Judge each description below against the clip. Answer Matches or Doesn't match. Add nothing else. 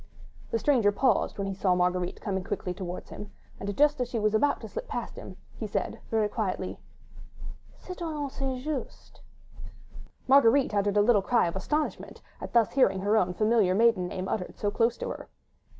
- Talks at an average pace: Matches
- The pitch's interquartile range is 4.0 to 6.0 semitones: Matches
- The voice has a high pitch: Matches